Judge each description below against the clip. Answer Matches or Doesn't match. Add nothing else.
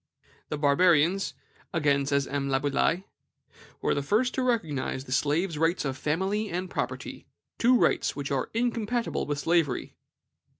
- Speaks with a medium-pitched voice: Matches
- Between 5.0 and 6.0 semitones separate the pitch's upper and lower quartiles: Matches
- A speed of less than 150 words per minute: Matches